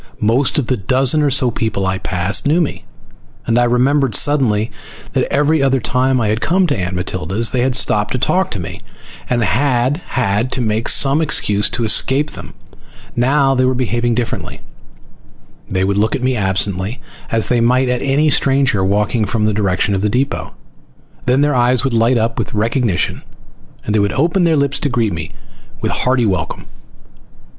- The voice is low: Yes, low, 120 Hz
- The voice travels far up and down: No, average, 4.3 semitones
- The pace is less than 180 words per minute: No, average, 190 wpm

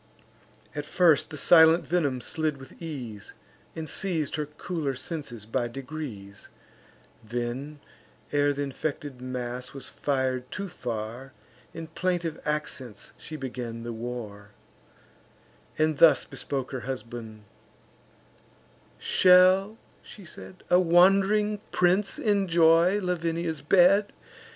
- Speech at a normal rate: No, slow, 110 wpm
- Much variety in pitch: Yes, wide, 5.7 semitones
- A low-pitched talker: No, medium, 150 Hz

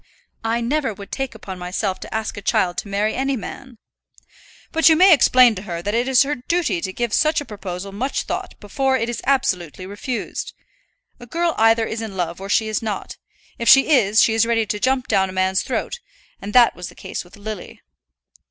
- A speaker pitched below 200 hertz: No, high, 225 Hz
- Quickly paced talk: Yes, fast, 215 wpm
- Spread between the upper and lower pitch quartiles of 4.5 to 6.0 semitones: Yes, average, 4.8 semitones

